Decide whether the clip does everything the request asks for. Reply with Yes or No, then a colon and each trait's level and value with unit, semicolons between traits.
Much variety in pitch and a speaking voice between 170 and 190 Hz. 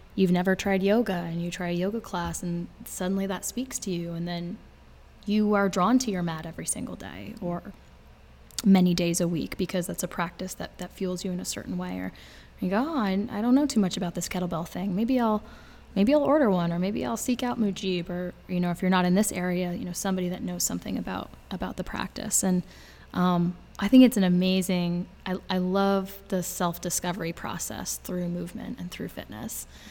No: narrow, 2.5 semitones; medium, 185 Hz